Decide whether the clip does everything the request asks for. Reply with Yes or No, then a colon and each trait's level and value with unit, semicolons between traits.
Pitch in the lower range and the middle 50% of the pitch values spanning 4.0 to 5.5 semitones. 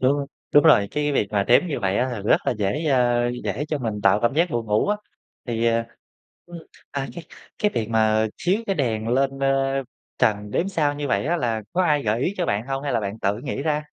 Yes: low, 130 Hz; average, 5.1 semitones